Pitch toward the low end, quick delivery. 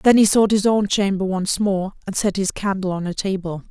No: high, 195 Hz; fast, 245 wpm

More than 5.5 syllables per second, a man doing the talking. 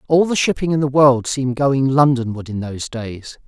No: 5.2 syllables/s; male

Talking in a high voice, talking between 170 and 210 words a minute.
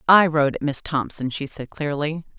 No: medium, 145 Hz; average, 200 wpm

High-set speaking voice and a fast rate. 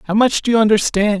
Yes: high, 215 Hz; fast, 250 wpm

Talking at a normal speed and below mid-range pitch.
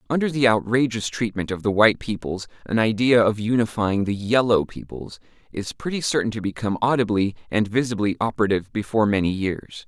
Yes: average, 165 wpm; low, 110 Hz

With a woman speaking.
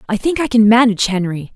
Yes: female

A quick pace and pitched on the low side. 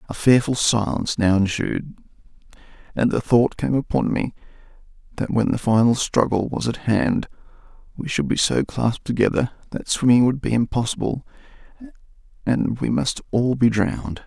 No: average, 150 wpm; low, 120 Hz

